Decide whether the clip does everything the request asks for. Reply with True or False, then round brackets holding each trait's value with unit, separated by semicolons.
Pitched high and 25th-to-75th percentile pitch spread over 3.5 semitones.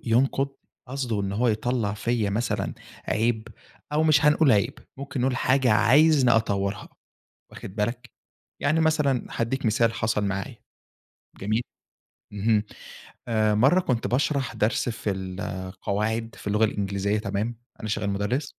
False (115 Hz; 3.9 semitones)